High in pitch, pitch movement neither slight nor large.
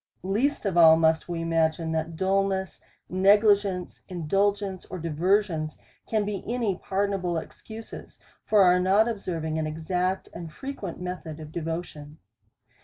No: medium, 180 Hz; average, 3.6 semitones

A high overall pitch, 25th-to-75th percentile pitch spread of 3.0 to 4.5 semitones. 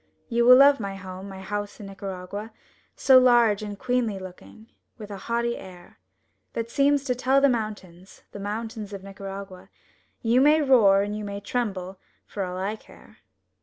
Yes: high, 210 Hz; average, 3.5 semitones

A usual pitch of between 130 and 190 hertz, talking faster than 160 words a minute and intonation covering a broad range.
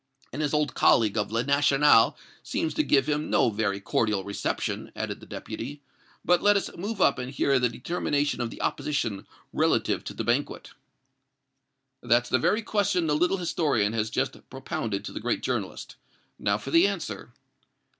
Yes: medium, 140 Hz; average, 175 wpm; wide, 6.1 semitones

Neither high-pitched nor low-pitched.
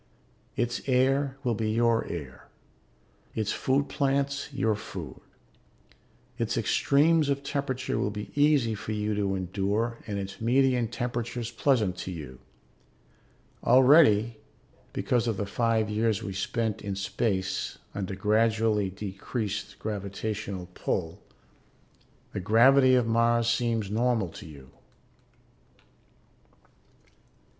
No: low, 110 Hz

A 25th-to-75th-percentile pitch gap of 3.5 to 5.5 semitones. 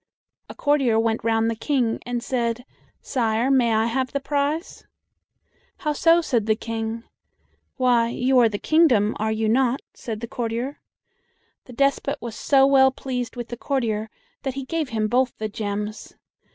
No: average, 3.1 semitones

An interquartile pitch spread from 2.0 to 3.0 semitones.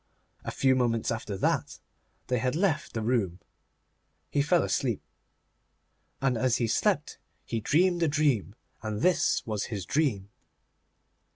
No: average, 5.1 semitones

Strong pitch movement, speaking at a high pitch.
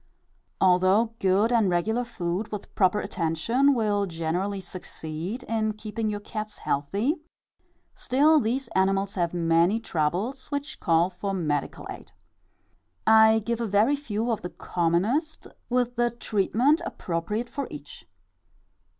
No: average, 4.7 semitones; high, 210 Hz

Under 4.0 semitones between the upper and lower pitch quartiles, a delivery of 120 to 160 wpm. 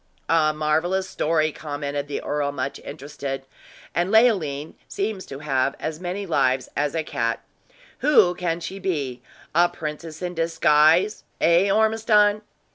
No: average, 4.3 semitones; slow, 135 wpm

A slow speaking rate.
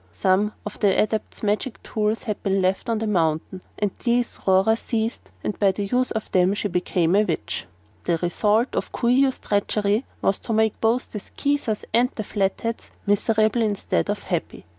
No: average, 185 wpm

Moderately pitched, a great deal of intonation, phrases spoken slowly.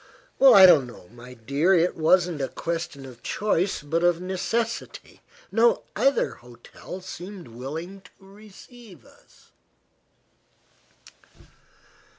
Yes: medium, 175 Hz; wide, 5.7 semitones; slow, 110 wpm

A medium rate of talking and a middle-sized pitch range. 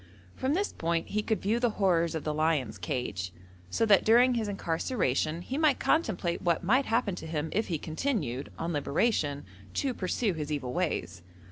No: average, 180 wpm; wide, 6.8 semitones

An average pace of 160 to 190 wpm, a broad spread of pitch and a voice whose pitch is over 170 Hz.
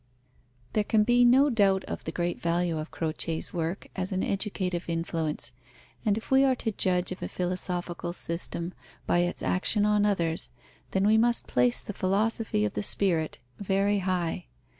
No: average, 170 wpm; average, 3.6 semitones; medium, 185 Hz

